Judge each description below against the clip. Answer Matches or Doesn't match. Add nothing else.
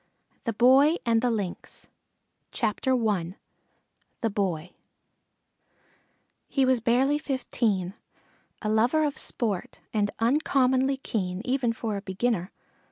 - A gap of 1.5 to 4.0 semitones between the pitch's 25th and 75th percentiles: Doesn't match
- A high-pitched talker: Matches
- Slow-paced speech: Matches